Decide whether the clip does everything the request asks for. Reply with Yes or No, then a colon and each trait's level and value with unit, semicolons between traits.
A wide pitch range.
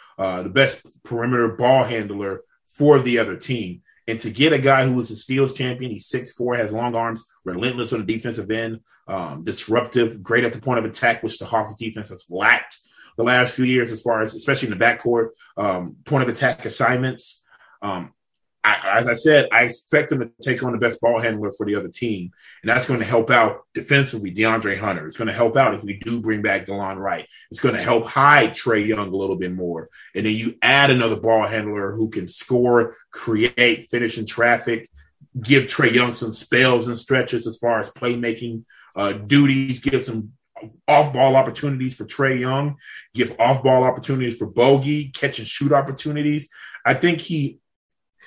No: average, 2.9 semitones